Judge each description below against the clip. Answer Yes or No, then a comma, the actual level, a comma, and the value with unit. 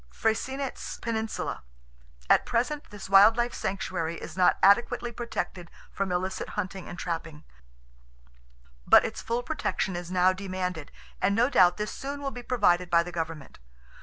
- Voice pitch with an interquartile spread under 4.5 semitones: No, average, 5.0 semitones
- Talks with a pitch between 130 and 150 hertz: No, high, 190 Hz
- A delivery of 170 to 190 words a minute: No, average, 145 wpm